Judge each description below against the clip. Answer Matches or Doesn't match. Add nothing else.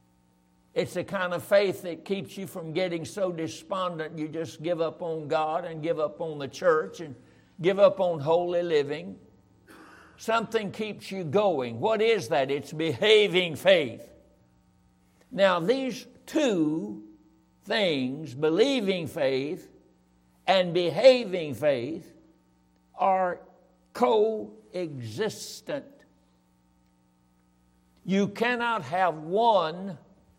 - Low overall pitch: Doesn't match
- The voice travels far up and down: Matches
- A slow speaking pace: Matches